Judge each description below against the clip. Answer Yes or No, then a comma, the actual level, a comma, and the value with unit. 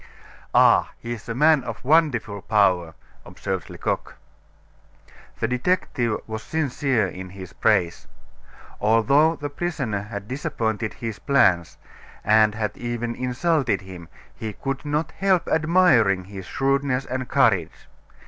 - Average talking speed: No, slow, 120 wpm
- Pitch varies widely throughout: Yes, wide, 5.7 semitones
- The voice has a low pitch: Yes, low, 120 Hz